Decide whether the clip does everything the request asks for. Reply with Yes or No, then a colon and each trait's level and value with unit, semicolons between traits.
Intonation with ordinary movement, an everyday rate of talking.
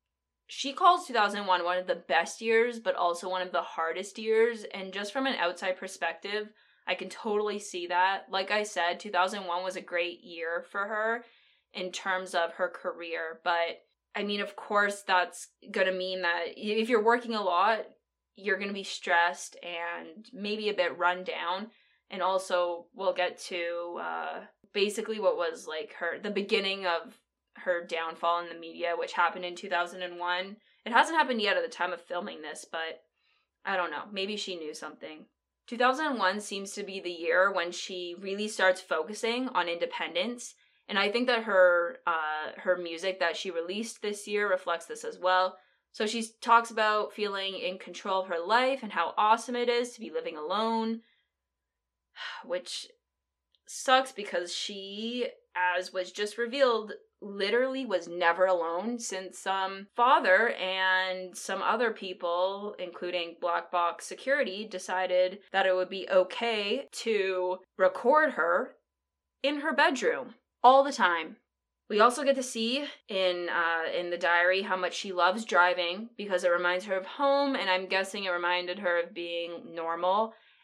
Yes: average, 4.1 semitones; average, 175 wpm